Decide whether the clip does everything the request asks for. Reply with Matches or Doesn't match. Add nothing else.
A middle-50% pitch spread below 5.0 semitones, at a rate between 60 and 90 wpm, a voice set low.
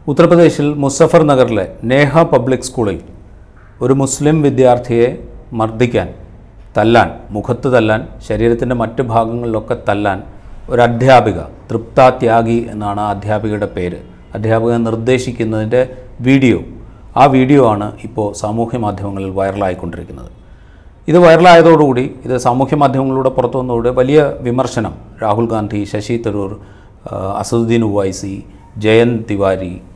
Doesn't match